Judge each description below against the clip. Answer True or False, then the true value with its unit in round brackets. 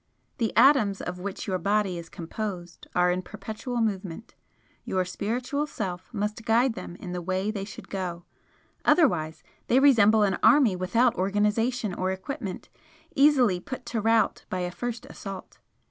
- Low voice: False (205 Hz)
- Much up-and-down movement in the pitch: False (4.2 semitones)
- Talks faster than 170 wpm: False (155 wpm)